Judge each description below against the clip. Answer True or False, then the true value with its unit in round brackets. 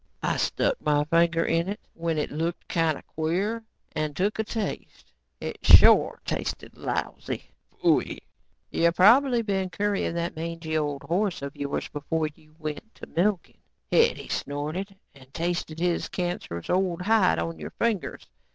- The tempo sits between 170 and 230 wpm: False (145 wpm)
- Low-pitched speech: False (170 Hz)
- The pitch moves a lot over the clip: False (4.0 semitones)